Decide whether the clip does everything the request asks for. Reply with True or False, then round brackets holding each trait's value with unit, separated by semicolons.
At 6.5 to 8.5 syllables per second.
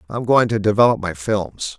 False (5.6 syllables/s)